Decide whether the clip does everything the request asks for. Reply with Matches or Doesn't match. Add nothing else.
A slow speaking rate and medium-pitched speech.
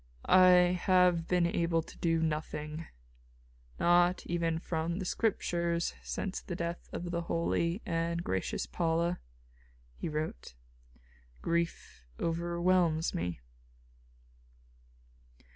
Matches